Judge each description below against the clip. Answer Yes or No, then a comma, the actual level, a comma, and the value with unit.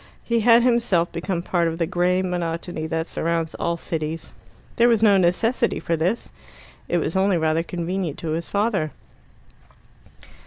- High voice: No, medium, 175 Hz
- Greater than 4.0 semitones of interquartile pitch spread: No, average, 3.3 semitones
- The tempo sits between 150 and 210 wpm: Yes, average, 155 wpm